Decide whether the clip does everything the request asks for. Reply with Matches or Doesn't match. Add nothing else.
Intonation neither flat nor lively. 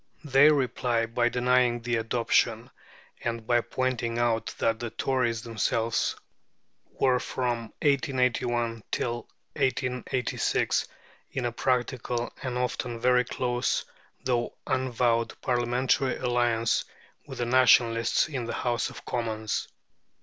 Doesn't match